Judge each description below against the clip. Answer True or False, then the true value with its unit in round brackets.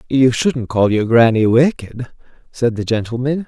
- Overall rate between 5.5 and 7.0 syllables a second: False (4.5 syllables/s)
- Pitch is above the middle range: False (125 Hz)